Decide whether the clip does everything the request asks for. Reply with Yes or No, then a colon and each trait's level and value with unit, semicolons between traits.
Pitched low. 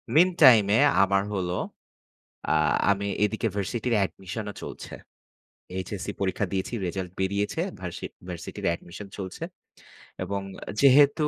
Yes: low, 100 Hz